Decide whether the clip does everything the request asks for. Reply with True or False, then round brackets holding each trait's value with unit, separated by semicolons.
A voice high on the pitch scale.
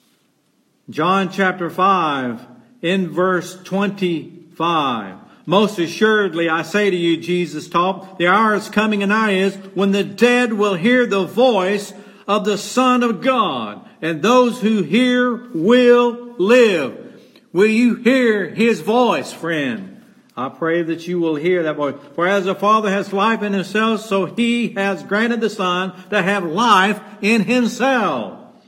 True (200 Hz)